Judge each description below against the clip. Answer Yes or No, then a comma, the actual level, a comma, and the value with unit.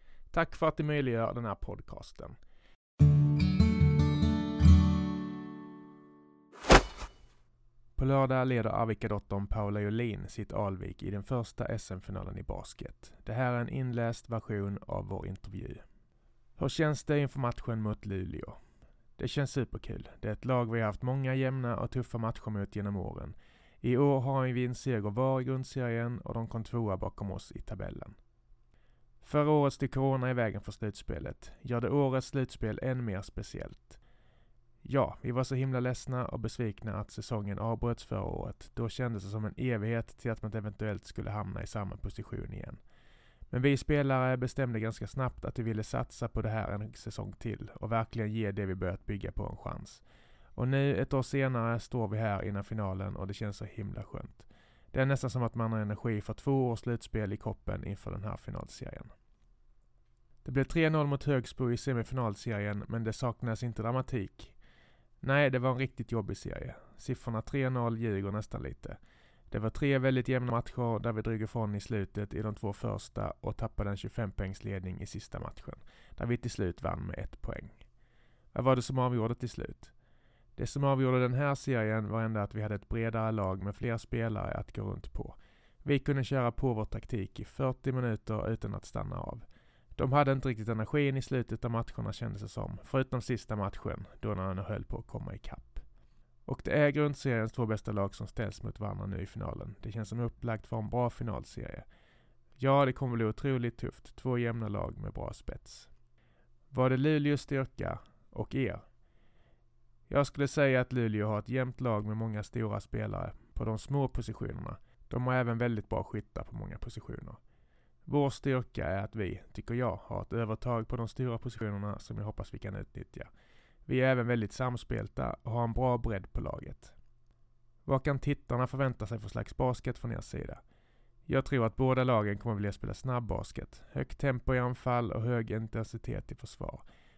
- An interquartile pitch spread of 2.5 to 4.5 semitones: Yes, average, 3.4 semitones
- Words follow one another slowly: No, average, 185 wpm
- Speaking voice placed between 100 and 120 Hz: Yes, low, 115 Hz